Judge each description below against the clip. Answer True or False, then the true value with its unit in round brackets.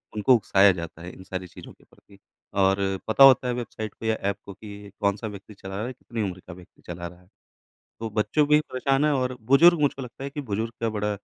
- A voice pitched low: True (110 Hz)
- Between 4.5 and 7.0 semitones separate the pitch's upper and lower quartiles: True (4.8 semitones)